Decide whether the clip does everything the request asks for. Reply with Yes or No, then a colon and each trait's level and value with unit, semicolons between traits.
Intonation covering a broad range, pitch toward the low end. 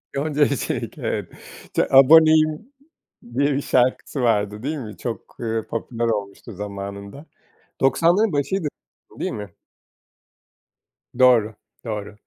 Yes: wide, 5.8 semitones; low, 125 Hz